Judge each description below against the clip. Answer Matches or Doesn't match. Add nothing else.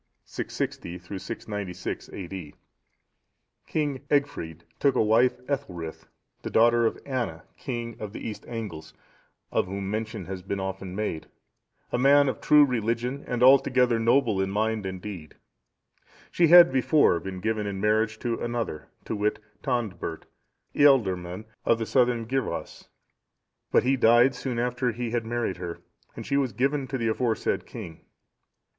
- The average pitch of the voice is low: Matches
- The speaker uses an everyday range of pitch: Matches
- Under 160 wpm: Matches